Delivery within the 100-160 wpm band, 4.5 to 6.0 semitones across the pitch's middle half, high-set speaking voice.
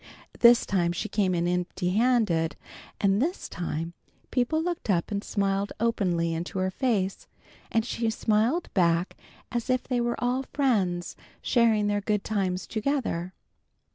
Yes: average, 145 wpm; average, 4.9 semitones; high, 205 Hz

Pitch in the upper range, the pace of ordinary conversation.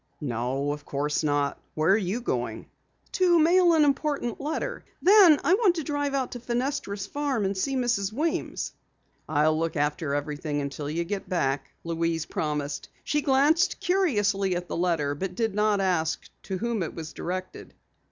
Yes: high, 195 Hz; average, 170 wpm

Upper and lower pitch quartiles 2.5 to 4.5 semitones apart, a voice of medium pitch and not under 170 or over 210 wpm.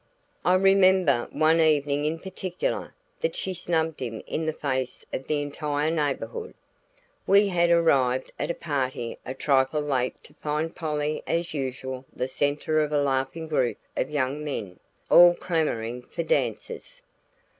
No: average, 4.0 semitones; medium, 150 Hz; average, 150 wpm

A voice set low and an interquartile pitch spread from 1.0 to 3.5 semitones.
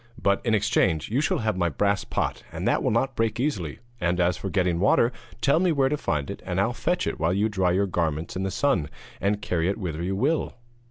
No: low, 100 Hz; average, 4.6 semitones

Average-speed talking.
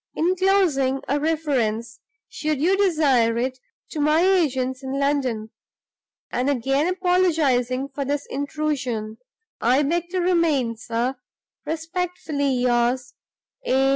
No: slow, 110 wpm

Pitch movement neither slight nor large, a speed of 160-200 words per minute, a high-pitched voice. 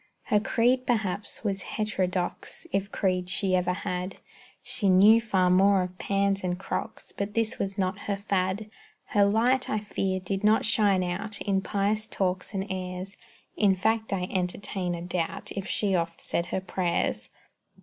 No: narrow, 2.3 semitones; average, 165 wpm; high, 195 Hz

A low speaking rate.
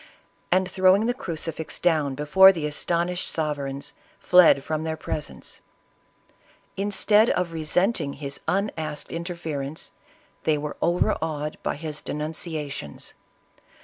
Yes: slow, 115 wpm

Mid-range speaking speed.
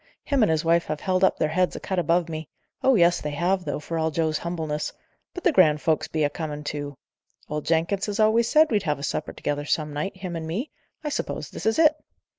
No: fast, 240 wpm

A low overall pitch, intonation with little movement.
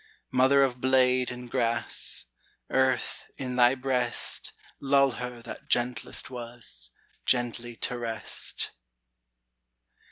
Yes: low, 125 Hz; narrow, 1.5 semitones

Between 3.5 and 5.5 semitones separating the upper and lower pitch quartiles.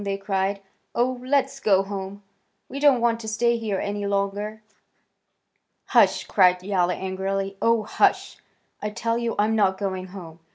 No: average, 3.0 semitones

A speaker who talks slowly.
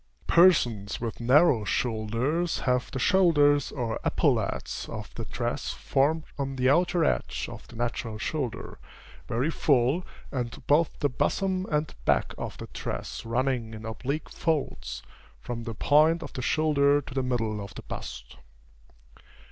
No: average, 150 wpm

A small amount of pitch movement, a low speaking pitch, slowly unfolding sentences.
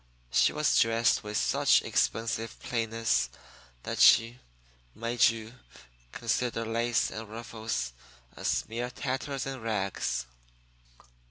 Yes: narrow, 1.3 semitones; low, 115 Hz; slow, 105 wpm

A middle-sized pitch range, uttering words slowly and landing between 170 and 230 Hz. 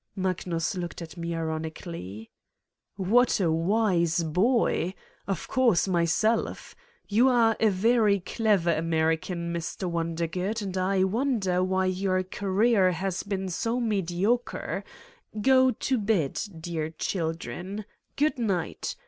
Yes: average, 4.3 semitones; slow, 115 wpm; medium, 185 Hz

